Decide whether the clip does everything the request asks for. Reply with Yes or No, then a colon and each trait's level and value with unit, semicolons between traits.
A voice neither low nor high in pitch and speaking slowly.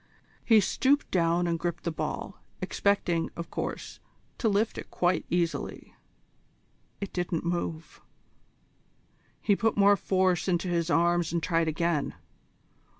Yes: medium, 175 Hz; slow, 130 wpm